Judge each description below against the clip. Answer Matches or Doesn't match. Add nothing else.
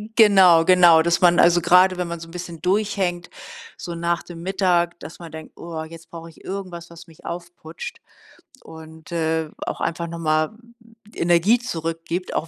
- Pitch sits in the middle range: Matches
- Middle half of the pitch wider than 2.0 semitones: Doesn't match